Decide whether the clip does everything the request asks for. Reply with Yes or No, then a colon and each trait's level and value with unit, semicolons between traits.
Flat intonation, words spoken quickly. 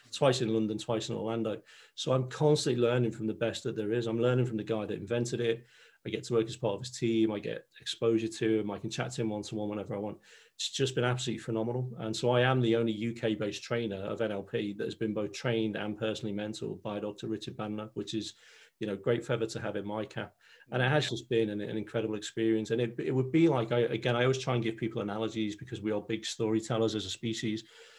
Yes: narrow, 1.8 semitones; fast, 255 wpm